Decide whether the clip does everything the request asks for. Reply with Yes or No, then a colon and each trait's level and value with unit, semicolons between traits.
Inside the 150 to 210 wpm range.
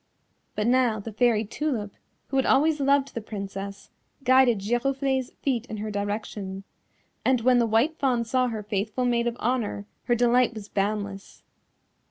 Yes: average, 160 wpm